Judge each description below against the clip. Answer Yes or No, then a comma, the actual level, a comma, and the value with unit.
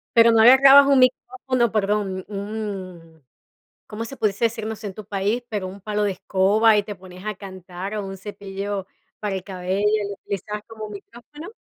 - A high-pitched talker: Yes, high, 205 Hz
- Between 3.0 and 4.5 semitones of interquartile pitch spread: No, narrow, 2.5 semitones